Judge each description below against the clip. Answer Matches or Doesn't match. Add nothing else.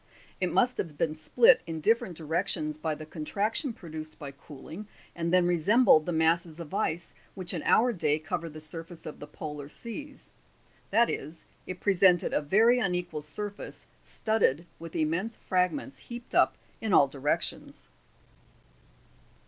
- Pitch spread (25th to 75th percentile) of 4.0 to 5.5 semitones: Matches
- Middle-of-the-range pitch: Matches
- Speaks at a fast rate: Doesn't match